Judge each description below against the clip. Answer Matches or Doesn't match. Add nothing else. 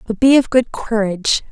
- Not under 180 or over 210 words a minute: Matches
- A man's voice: Doesn't match